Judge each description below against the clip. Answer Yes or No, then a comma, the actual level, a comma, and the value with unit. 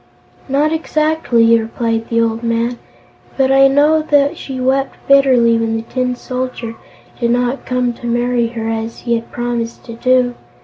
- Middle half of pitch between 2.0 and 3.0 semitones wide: Yes, narrow, 2.6 semitones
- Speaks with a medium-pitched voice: No, high, 245 Hz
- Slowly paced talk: No, average, 165 wpm